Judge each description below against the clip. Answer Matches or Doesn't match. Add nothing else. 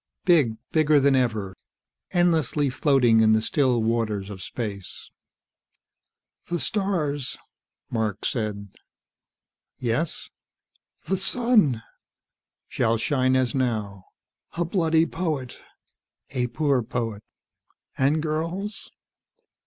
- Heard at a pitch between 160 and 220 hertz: Doesn't match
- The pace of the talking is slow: Matches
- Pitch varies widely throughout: Matches